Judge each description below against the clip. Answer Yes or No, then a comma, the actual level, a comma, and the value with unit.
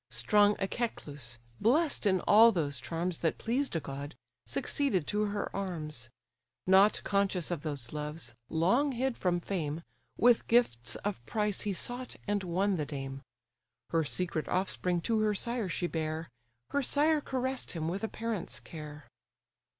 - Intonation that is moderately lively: No, wide, 6.1 semitones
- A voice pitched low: No, medium, 185 Hz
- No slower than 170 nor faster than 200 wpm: No, average, 150 wpm